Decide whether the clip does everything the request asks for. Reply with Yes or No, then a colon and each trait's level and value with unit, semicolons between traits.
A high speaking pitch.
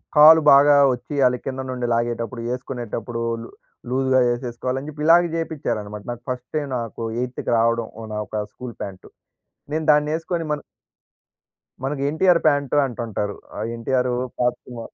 No: low, 125 Hz